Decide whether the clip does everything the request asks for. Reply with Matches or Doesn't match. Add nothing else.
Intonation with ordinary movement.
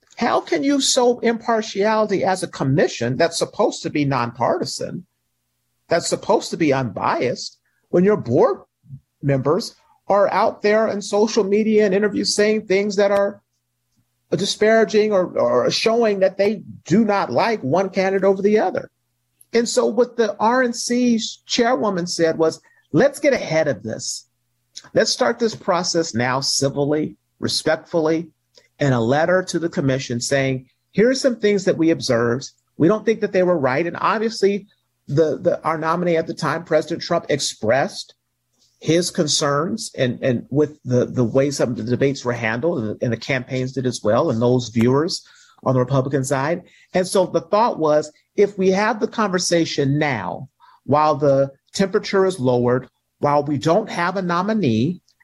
Doesn't match